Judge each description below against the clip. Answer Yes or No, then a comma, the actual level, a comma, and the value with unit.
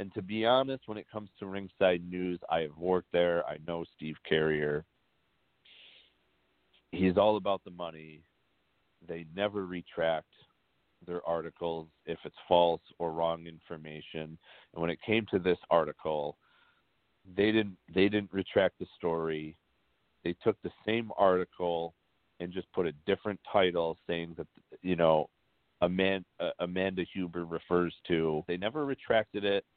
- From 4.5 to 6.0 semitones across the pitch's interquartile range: No, average, 3.1 semitones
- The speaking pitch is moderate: No, very low, 90 Hz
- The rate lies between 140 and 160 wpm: Yes, average, 145 wpm